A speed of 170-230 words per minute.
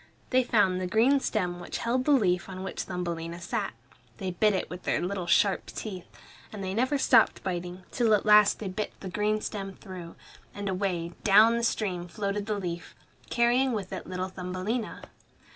Yes: average, 185 wpm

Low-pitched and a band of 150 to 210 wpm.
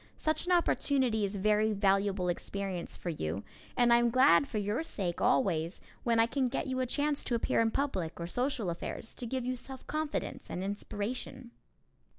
No: high, 230 Hz; average, 185 wpm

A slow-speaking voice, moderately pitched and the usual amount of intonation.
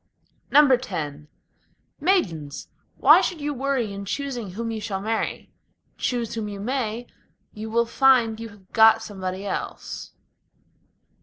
No: slow, 130 wpm; high, 225 Hz; average, 4.4 semitones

